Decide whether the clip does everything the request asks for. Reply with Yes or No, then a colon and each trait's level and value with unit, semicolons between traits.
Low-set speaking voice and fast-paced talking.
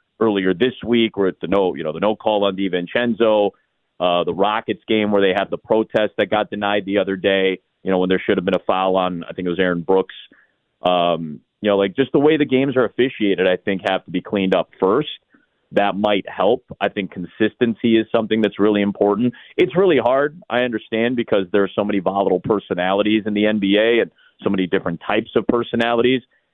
Yes: low, 100 Hz; fast, 215 wpm